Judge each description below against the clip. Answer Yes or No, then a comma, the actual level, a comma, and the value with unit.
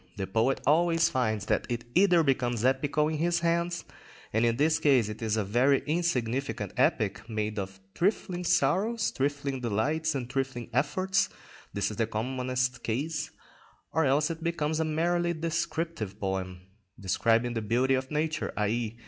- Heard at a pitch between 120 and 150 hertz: Yes, low, 135 Hz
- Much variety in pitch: Yes, wide, 5.9 semitones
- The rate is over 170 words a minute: No, average, 155 wpm